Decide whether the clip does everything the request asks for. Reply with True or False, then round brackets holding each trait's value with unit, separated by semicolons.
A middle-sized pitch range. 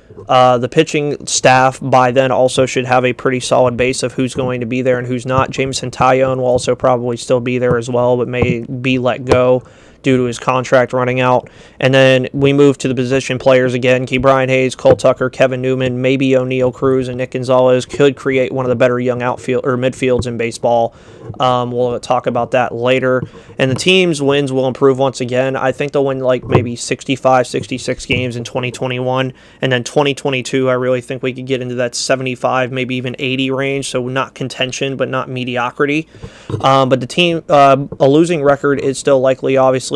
False (1.0 semitones)